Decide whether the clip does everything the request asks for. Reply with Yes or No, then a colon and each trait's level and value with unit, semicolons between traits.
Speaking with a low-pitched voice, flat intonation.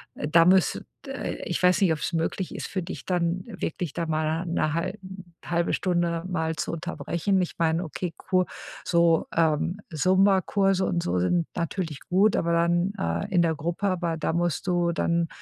No: medium, 170 Hz; narrow, 2.0 semitones